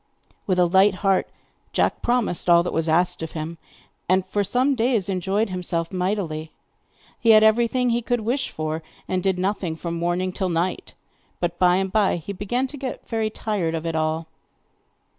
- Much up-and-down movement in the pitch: No, average, 4.3 semitones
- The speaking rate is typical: Yes, average, 180 wpm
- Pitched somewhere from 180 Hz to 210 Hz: Yes, medium, 185 Hz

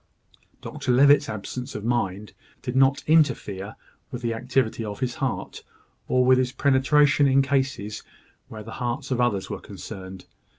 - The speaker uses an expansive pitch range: No, average, 3.8 semitones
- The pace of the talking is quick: No, average, 155 wpm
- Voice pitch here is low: Yes, low, 125 Hz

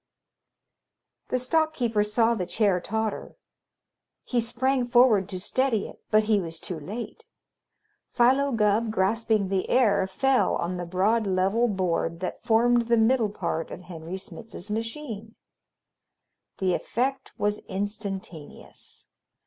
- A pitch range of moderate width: Yes, average, 3.9 semitones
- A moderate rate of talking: No, slow, 130 wpm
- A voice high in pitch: Yes, high, 215 Hz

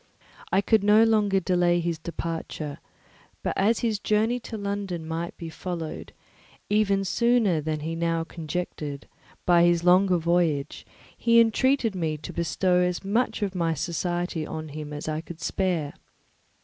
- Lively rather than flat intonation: No, average, 3.7 semitones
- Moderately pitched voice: Yes, medium, 175 Hz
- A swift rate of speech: No, average, 155 wpm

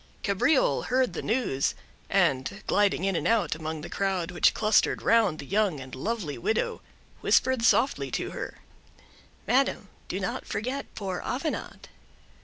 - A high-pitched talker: Yes, high, 200 Hz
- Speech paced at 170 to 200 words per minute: No, average, 140 wpm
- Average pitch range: No, wide, 6.2 semitones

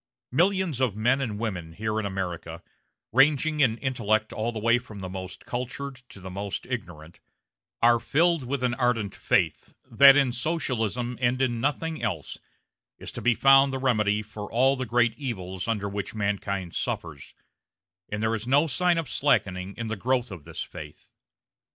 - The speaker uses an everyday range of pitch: Yes, average, 4.6 semitones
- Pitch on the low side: Yes, low, 115 Hz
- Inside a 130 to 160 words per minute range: No, average, 175 wpm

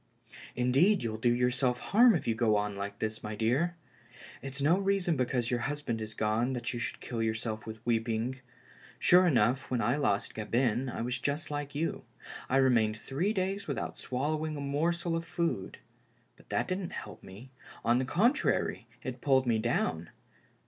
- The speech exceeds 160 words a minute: Yes, average, 175 wpm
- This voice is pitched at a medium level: No, low, 125 Hz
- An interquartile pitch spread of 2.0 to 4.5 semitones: No, average, 5.1 semitones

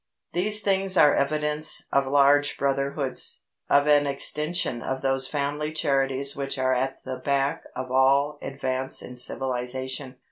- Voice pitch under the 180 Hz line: Yes, medium, 140 Hz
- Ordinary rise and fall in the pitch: No, narrow, 1.8 semitones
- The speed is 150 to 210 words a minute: No, average, 140 wpm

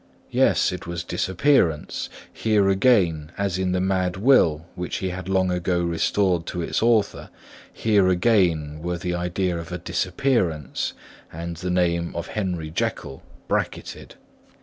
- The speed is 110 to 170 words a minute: Yes, average, 145 wpm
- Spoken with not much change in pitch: Yes, narrow, 2.2 semitones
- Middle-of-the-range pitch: No, very low, 90 Hz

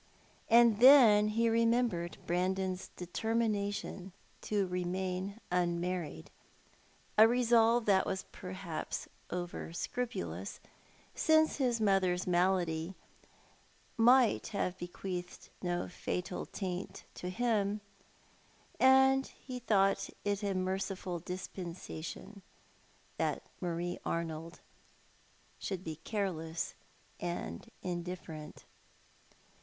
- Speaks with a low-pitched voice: No, high, 190 Hz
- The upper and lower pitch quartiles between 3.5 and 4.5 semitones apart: Yes, average, 3.9 semitones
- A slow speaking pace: Yes, slow, 95 wpm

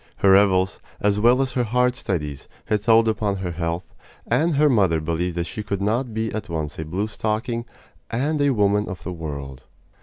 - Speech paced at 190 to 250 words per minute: Yes, average, 200 wpm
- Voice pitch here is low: Yes, low, 105 Hz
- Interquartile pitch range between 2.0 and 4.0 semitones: No, average, 5.0 semitones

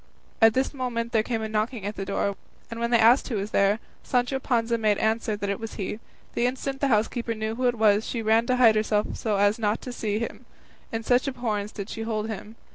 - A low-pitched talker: No, high, 225 Hz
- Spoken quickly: Yes, fast, 240 wpm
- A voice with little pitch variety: Yes, narrow, 2.1 semitones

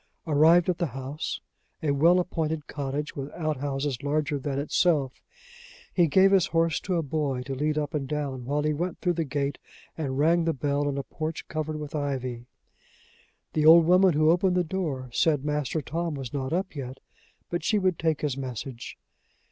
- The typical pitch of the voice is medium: Yes, medium, 150 Hz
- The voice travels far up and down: No, average, 3.0 semitones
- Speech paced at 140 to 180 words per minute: No, average, 190 wpm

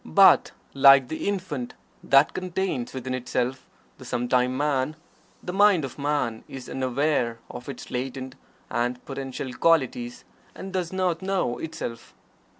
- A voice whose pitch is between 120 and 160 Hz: Yes, low, 135 Hz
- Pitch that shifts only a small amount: No, average, 4.6 semitones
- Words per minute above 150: No, slow, 135 wpm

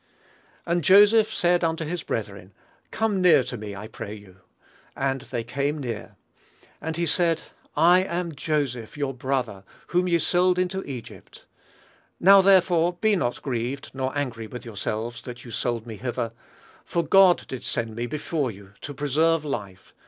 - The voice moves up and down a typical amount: No, wide, 6.6 semitones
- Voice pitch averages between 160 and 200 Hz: No, medium, 140 Hz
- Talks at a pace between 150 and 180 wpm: Yes, average, 160 wpm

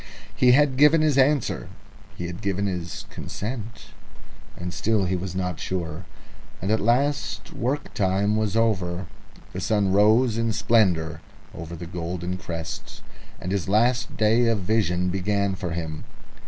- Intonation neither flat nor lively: Yes, average, 4.3 semitones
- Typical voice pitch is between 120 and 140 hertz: No, low, 100 Hz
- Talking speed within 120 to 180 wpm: Yes, average, 150 wpm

